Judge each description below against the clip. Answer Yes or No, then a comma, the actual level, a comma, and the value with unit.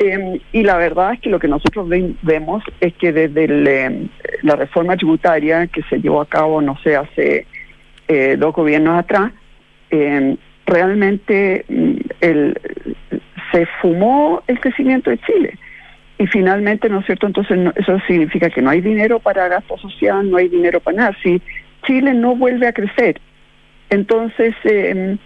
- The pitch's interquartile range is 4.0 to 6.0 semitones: Yes, average, 4.3 semitones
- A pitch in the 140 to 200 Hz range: Yes, high, 190 Hz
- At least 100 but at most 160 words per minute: Yes, average, 155 wpm